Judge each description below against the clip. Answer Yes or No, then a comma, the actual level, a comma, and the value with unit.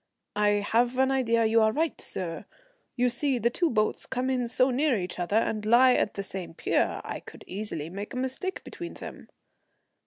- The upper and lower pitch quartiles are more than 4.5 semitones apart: No, average, 4.0 semitones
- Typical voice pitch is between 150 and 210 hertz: No, high, 235 Hz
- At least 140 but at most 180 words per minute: No, average, 195 wpm